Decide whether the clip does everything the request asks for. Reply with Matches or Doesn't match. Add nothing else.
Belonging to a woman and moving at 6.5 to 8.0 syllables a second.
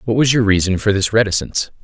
Doesn't match